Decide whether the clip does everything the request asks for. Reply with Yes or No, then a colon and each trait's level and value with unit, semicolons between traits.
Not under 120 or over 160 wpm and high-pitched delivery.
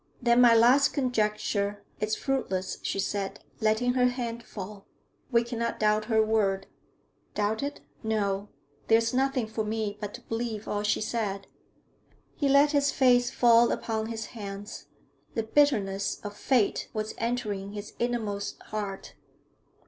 Yes: average, 145 wpm; high, 220 Hz